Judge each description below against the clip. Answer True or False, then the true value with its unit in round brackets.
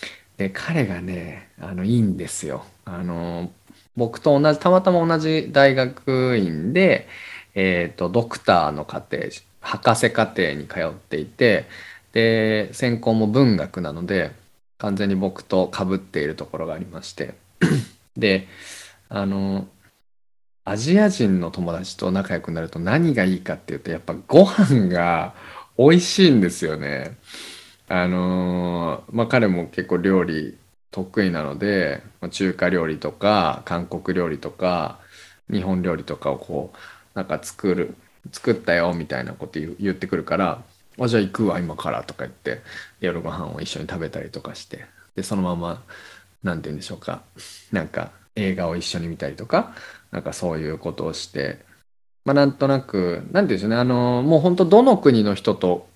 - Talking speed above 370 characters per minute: False (300 characters per minute)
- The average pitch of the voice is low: True (95 Hz)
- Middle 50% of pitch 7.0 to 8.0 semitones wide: False (5.3 semitones)